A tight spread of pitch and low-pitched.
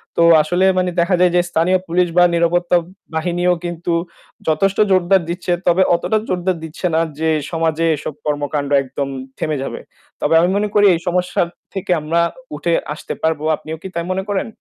No: narrow, 2.0 semitones; medium, 175 Hz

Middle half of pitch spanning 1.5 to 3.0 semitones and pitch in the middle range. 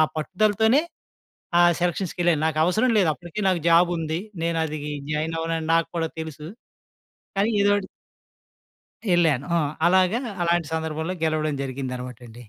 Yes: average, 2.7 semitones; medium, 165 Hz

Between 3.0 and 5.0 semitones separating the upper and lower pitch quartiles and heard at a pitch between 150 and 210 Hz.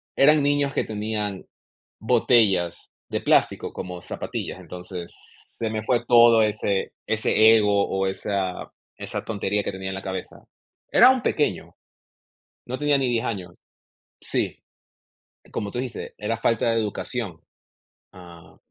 No: average, 3.7 semitones; low, 105 Hz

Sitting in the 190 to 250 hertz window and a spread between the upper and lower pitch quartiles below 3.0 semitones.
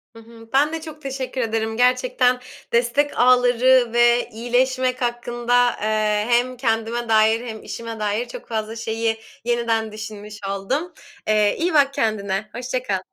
Yes: high, 235 Hz; narrow, 2.4 semitones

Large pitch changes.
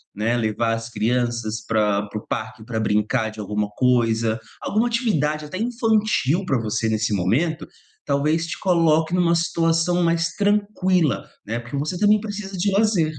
Yes: wide, 8.3 semitones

